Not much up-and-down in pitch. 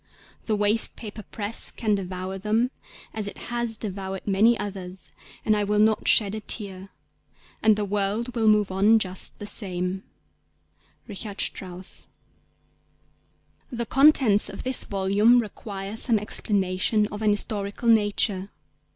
Yes: narrow, 2.2 semitones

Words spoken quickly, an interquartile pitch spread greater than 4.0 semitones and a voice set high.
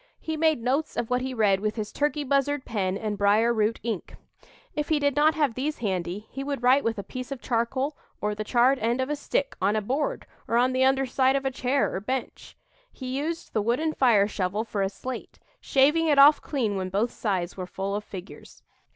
Yes: fast, 225 wpm; average, 4.9 semitones; very high, 250 Hz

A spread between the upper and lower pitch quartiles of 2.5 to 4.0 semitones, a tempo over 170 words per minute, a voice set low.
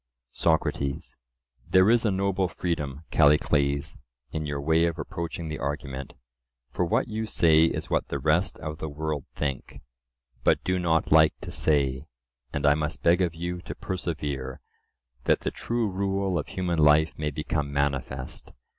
No: average, 3.5 semitones; average, 160 wpm; very low, 80 Hz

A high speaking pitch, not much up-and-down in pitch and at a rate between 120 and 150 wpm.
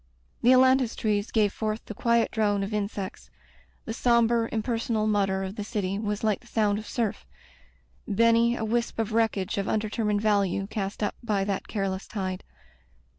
No: high, 215 Hz; narrow, 2.3 semitones; average, 170 wpm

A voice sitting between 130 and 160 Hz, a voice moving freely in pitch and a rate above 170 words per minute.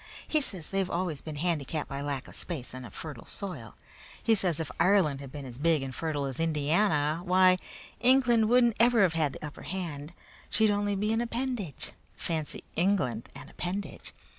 No: medium, 170 Hz; wide, 5.8 semitones; average, 185 wpm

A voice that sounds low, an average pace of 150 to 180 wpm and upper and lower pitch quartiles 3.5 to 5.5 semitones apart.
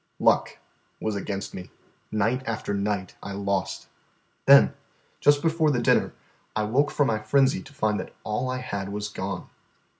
Yes: low, 105 Hz; average, 160 wpm; average, 4.6 semitones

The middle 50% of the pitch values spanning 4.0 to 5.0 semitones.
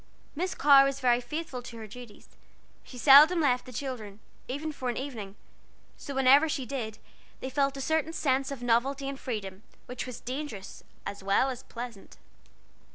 No: average, 2.9 semitones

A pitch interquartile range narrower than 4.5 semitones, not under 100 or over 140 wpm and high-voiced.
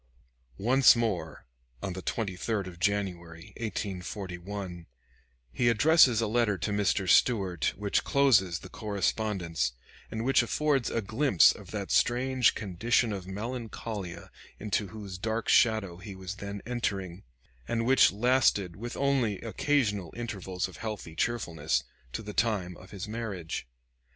No: average, 4.0 semitones; slow, 135 wpm; low, 105 Hz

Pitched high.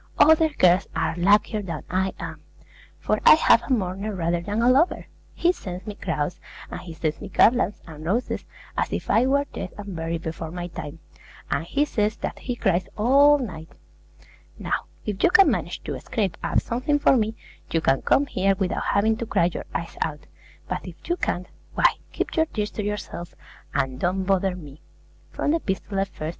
Yes: high, 195 Hz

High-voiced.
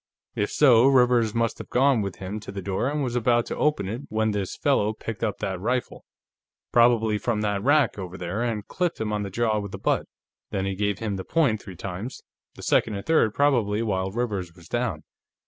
No: low, 110 Hz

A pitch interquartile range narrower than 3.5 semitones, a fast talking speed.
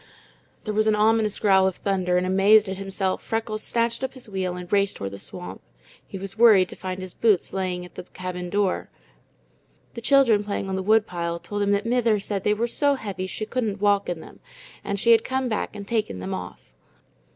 Yes: average, 2.8 semitones; fast, 215 wpm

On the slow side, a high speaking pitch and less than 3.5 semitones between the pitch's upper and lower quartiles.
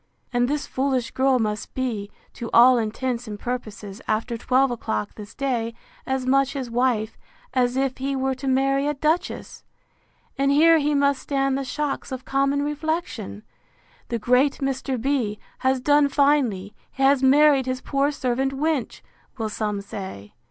No: average, 160 wpm; very high, 260 Hz; average, 2.9 semitones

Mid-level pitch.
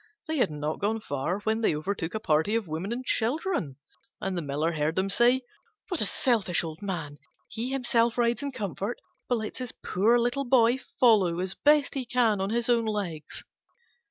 No: high, 215 Hz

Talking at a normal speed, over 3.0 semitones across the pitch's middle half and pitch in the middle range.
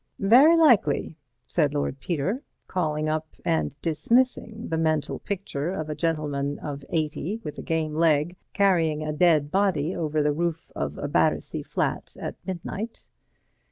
Yes: average, 150 wpm; average, 3.9 semitones; medium, 160 Hz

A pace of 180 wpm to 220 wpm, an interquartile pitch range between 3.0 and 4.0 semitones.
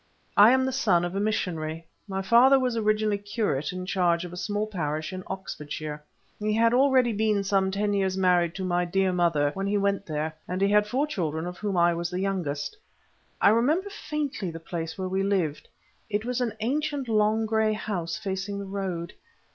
Yes: average, 200 wpm; average, 3.7 semitones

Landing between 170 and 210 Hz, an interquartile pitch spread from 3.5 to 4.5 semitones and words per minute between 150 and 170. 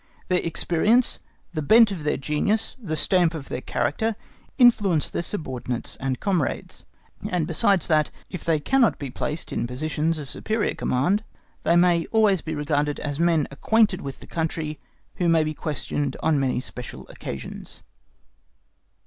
No: medium, 160 Hz; average, 4.1 semitones; average, 155 wpm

